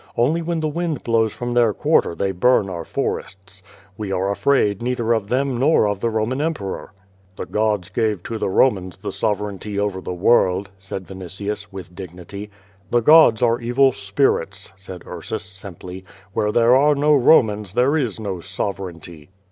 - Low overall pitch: Yes, low, 105 Hz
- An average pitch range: Yes, average, 4.2 semitones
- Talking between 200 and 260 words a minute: No, average, 170 wpm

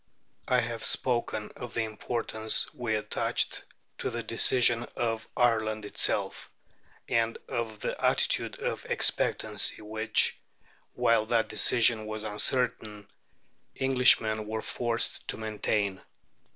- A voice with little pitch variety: Yes, narrow, 1.6 semitones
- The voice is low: Yes, low, 110 Hz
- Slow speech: Yes, slow, 110 wpm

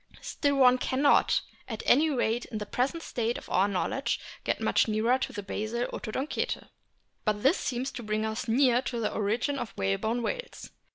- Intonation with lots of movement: No, average, 3.5 semitones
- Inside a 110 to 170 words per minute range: No, average, 190 wpm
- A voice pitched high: Yes, high, 240 Hz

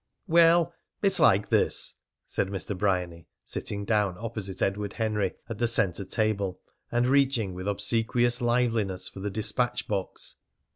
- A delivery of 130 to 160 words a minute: Yes, average, 140 wpm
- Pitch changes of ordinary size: Yes, average, 3.6 semitones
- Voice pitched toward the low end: Yes, low, 105 Hz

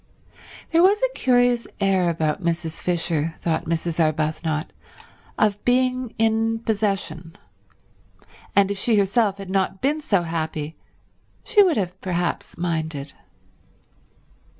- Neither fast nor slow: No, slow, 120 wpm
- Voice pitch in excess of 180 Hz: Yes, high, 190 Hz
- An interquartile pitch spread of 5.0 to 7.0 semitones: Yes, wide, 5.5 semitones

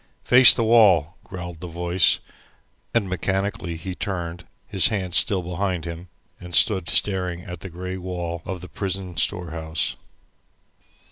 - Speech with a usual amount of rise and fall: No, narrow, 1.9 semitones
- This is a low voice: Yes, very low, 90 Hz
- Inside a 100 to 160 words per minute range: Yes, average, 140 wpm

